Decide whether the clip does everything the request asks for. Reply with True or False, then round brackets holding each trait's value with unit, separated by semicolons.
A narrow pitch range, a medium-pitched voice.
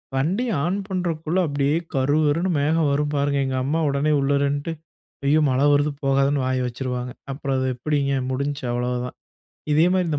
True (2.3 semitones; 145 Hz)